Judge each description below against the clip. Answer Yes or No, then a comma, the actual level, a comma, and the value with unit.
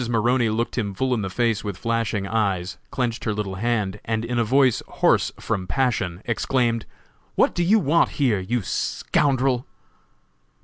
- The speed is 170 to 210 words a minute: Yes, average, 175 wpm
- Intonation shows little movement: No, average, 3.2 semitones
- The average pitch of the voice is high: No, low, 115 Hz